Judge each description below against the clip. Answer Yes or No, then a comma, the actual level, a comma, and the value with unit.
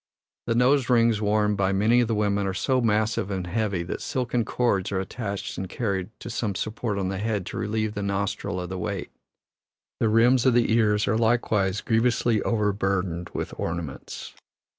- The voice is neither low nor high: No, low, 105 Hz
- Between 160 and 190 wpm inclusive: Yes, average, 185 wpm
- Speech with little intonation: No, average, 3.0 semitones